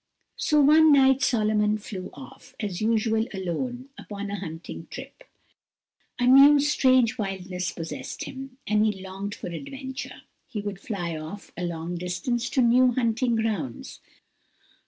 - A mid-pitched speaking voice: No, high, 215 Hz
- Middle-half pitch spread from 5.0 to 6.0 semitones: Yes, average, 5.3 semitones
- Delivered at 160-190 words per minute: No, average, 140 wpm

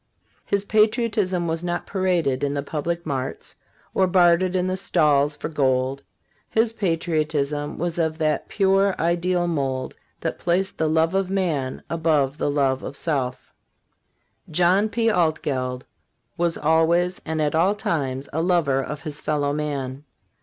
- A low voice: No, medium, 160 Hz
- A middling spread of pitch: Yes, average, 4.0 semitones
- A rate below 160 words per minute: Yes, average, 145 wpm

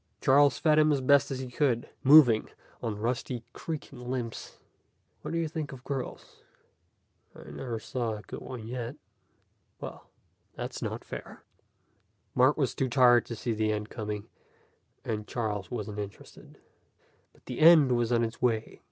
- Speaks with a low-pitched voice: Yes, low, 125 Hz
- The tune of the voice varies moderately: Yes, average, 3.3 semitones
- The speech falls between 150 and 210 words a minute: Yes, average, 155 wpm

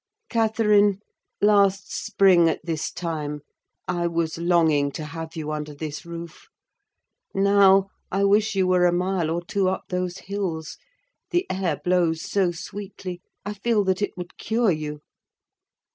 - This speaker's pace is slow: No, average, 145 wpm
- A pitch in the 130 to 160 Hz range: No, medium, 180 Hz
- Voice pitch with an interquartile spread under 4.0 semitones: Yes, average, 3.4 semitones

